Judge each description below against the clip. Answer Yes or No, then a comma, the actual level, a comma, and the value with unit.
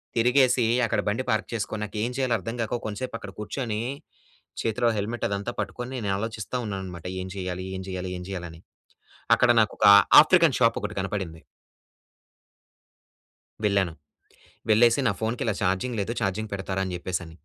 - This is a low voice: Yes, low, 105 Hz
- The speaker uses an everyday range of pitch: Yes, average, 3.6 semitones